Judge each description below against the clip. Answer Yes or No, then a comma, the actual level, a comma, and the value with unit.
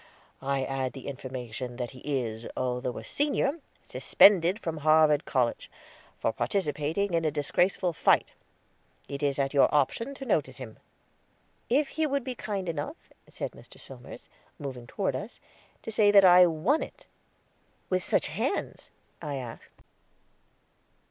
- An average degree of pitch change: No, wide, 7.1 semitones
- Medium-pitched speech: Yes, medium, 150 Hz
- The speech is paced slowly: No, average, 145 wpm